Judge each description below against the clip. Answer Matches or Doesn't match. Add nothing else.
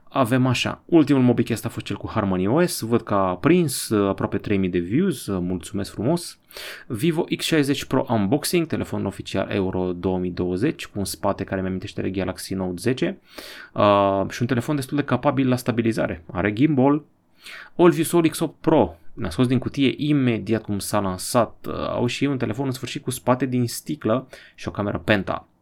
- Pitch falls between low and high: Doesn't match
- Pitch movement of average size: Doesn't match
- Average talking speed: Doesn't match